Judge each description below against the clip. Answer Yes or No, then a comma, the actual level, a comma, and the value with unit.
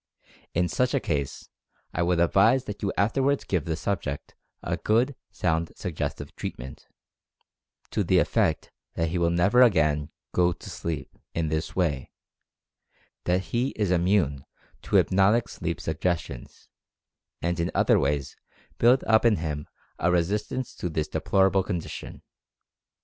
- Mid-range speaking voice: No, very low, 90 Hz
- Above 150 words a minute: No, average, 145 wpm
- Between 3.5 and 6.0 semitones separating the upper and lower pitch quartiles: Yes, average, 4.4 semitones